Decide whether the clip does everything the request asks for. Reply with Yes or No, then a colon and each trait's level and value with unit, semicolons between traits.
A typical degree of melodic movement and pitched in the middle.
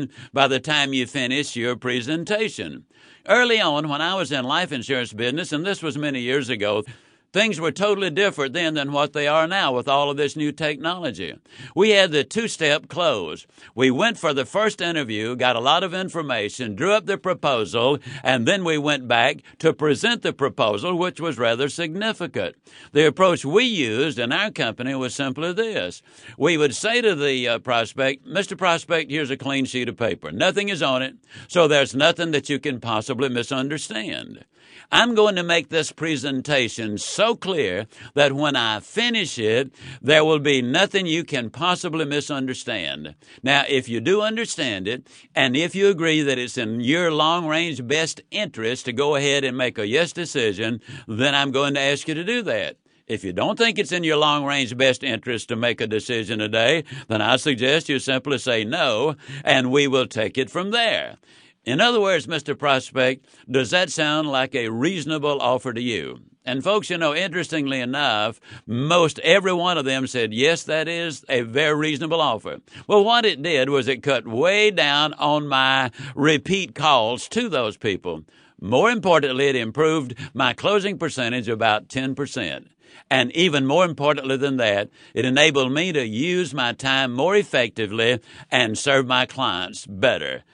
Yes: average, 4.7 semitones; medium, 145 Hz